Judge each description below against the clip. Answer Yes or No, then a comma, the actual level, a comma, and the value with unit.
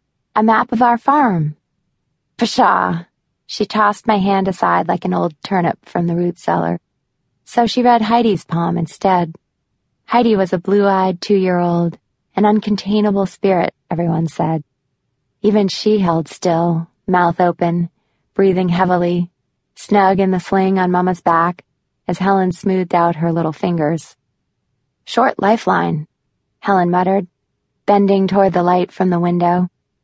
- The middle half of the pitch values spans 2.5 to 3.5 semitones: Yes, average, 2.9 semitones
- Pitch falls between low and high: Yes, medium, 180 Hz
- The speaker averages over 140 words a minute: No, slow, 135 wpm